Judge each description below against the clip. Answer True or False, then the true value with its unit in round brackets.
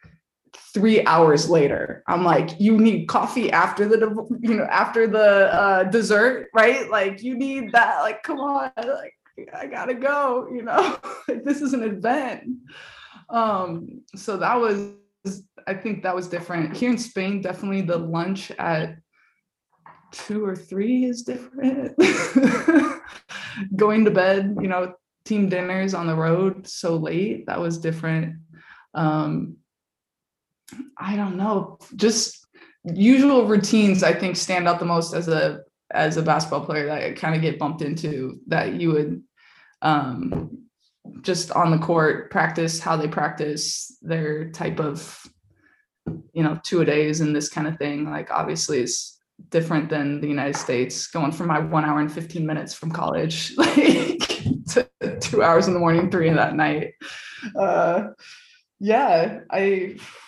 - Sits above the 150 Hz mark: True (190 Hz)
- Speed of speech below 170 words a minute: True (155 wpm)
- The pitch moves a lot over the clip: True (6.2 semitones)